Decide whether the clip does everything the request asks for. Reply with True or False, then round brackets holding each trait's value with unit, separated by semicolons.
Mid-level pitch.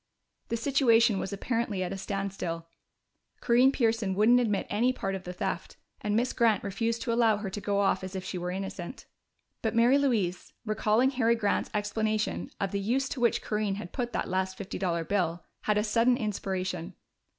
False (210 Hz)